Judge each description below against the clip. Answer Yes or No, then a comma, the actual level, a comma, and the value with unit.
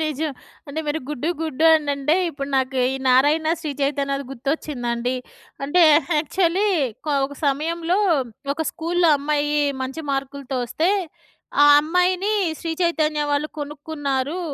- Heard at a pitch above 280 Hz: Yes, very high, 295 Hz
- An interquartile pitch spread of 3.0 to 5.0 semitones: No, narrow, 2.6 semitones